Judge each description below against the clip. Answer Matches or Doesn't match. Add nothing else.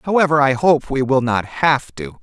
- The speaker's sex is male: Matches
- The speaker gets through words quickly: Matches